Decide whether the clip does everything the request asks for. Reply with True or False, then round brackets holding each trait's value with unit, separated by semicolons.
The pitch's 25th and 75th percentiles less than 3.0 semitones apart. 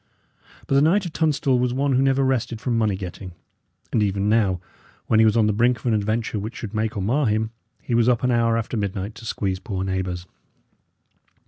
False (3.6 semitones)